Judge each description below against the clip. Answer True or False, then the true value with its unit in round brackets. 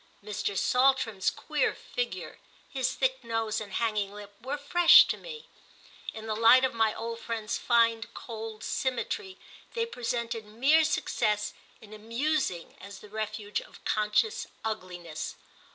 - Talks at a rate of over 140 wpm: False (135 wpm)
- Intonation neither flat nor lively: True (3.6 semitones)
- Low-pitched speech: False (225 Hz)